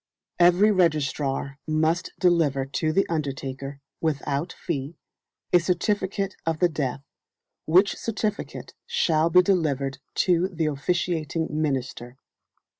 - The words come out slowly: Yes, slow, 110 wpm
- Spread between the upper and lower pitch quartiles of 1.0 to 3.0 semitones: No, average, 4.2 semitones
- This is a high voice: No, medium, 160 Hz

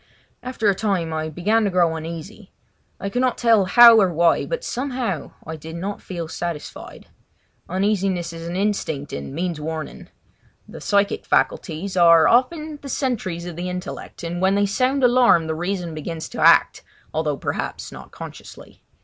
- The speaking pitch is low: No, medium, 185 Hz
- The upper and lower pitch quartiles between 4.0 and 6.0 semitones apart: Yes, average, 4.8 semitones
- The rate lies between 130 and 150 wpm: No, average, 165 wpm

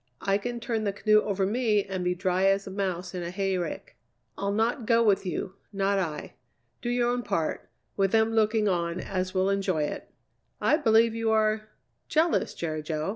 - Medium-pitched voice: No, high, 200 Hz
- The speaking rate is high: No, average, 190 wpm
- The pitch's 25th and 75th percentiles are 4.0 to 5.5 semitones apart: No, average, 3.2 semitones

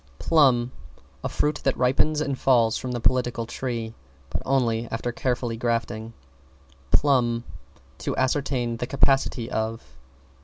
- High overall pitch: No, low, 120 Hz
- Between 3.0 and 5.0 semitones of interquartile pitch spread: No, narrow, 2.5 semitones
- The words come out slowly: Yes, slow, 125 wpm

